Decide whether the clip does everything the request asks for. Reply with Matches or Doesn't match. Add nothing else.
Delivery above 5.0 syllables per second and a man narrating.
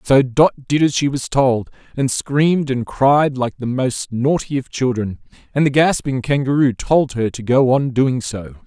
Doesn't match